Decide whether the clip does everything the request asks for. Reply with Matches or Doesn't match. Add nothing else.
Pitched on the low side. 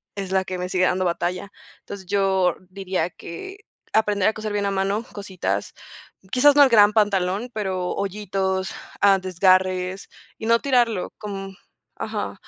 Doesn't match